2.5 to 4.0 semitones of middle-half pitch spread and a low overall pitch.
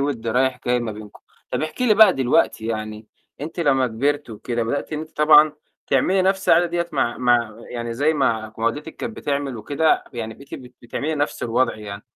No: average, 5.0 semitones; low, 130 Hz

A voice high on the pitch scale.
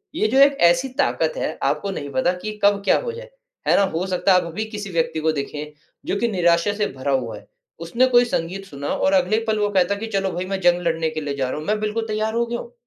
Yes: high, 195 Hz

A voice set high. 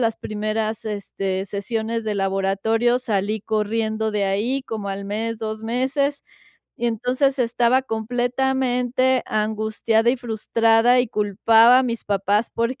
Yes: high, 225 Hz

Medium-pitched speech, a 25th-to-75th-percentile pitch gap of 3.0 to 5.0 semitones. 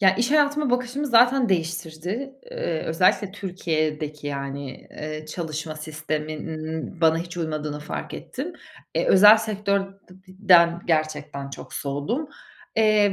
No: medium, 170 Hz; wide, 5.5 semitones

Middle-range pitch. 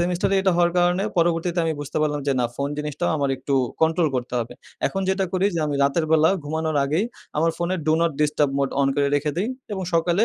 Yes: medium, 160 Hz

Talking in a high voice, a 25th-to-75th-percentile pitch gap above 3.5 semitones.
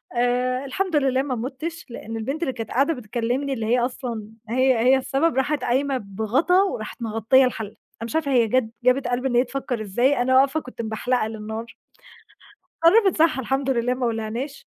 No: very high, 255 Hz; average, 2.9 semitones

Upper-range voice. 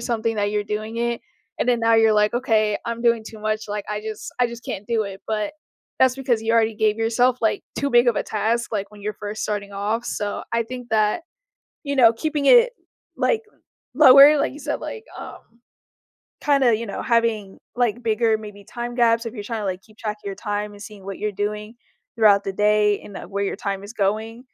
Yes: high, 220 Hz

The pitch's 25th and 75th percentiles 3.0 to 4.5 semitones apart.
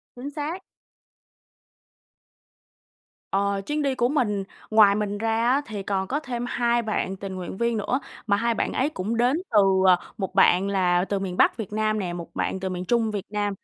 Yes: average, 3.6 semitones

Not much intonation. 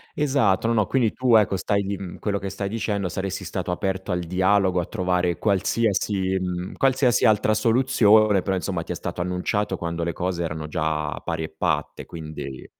No: average, 3.1 semitones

